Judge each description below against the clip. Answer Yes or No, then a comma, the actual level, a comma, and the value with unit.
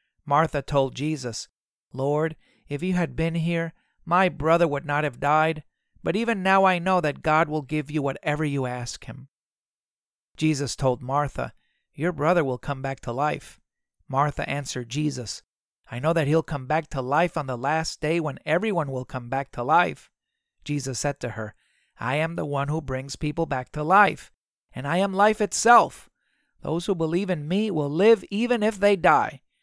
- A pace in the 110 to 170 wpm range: No, average, 185 wpm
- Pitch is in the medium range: Yes, medium, 150 Hz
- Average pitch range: Yes, average, 3.7 semitones